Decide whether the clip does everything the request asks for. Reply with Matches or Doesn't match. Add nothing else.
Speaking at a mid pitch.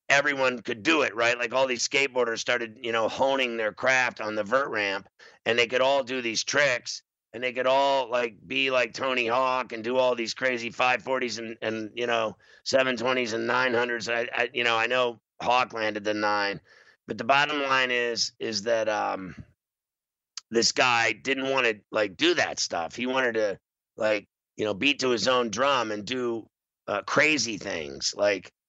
Doesn't match